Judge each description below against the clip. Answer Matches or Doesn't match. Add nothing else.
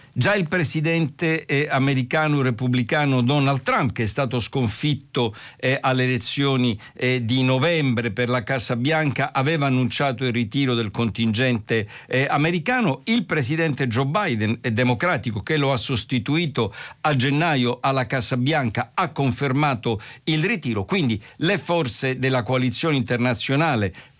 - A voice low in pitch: Matches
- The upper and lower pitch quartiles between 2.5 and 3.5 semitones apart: Matches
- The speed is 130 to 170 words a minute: Doesn't match